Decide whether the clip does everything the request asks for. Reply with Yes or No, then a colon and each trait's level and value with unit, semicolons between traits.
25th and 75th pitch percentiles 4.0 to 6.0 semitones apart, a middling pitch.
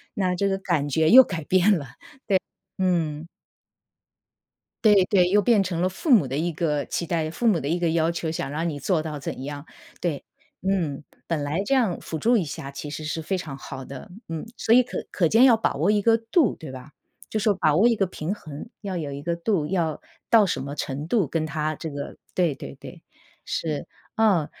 Yes: average, 4.6 semitones; medium, 170 Hz